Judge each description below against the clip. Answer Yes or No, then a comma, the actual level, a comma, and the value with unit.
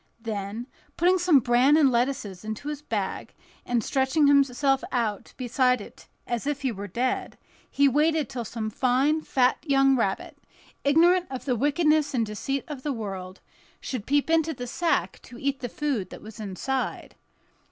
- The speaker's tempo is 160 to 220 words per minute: Yes, average, 165 wpm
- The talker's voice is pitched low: No, very high, 260 Hz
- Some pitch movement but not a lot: Yes, average, 4.1 semitones